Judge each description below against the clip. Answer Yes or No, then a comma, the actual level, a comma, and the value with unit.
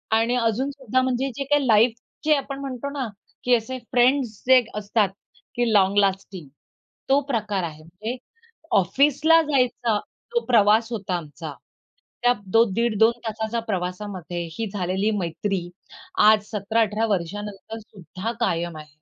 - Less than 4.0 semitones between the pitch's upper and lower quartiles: No, average, 4.4 semitones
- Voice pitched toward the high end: Yes, high, 220 Hz